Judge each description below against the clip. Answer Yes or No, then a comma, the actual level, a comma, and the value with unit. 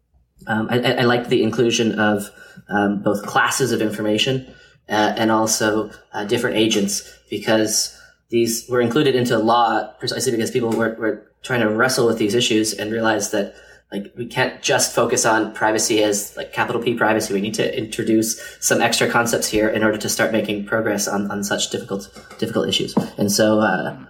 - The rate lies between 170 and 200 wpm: Yes, average, 180 wpm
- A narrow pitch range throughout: Yes, narrow, 1.7 semitones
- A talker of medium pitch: No, low, 110 Hz